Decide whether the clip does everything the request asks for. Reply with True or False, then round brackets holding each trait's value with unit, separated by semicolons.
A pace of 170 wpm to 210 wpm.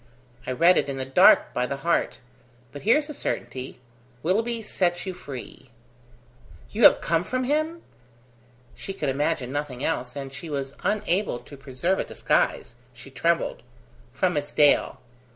False (155 wpm)